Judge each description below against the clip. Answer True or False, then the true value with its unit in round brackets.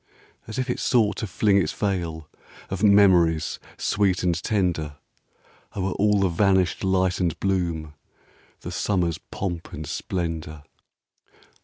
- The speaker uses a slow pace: True (130 wpm)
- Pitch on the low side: True (95 Hz)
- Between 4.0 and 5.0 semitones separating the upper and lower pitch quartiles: False (3.2 semitones)